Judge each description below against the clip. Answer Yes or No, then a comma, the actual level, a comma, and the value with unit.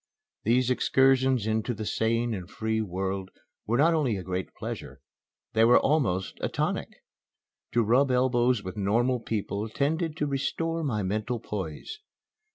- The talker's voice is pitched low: Yes, low, 115 Hz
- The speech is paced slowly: No, average, 150 wpm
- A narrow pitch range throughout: No, average, 4.2 semitones